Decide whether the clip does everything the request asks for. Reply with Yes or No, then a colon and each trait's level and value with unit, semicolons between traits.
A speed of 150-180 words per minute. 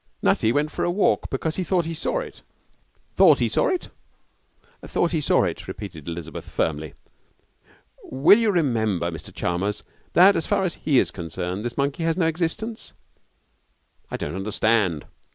Yes: average, 165 wpm